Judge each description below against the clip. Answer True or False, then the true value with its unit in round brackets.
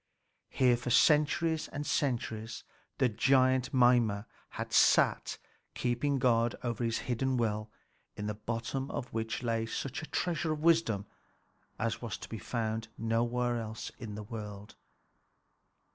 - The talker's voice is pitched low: True (120 Hz)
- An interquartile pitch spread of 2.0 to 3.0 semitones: True (2.7 semitones)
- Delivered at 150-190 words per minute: False (140 wpm)